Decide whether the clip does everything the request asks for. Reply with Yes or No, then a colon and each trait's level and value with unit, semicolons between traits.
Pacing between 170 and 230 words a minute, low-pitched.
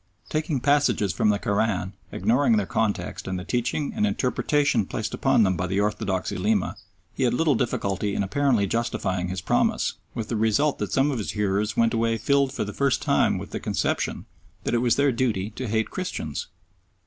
Yes: average, 195 wpm; low, 110 Hz